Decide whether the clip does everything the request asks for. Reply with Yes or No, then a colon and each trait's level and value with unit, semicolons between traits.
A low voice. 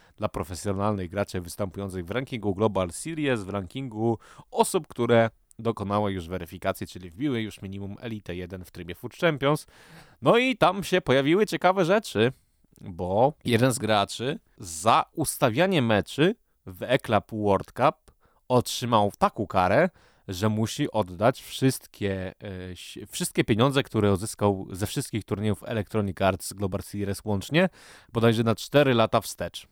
Yes: low, 110 Hz